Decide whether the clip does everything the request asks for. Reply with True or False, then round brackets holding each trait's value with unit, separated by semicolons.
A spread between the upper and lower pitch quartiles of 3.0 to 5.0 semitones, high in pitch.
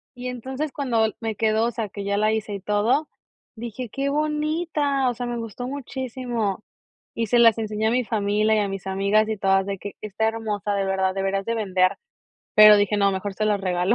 True (3.4 semitones; 220 Hz)